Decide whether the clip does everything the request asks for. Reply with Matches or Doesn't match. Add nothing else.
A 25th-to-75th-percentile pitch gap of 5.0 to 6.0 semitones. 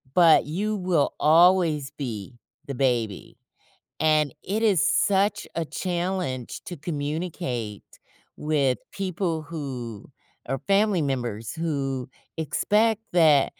Matches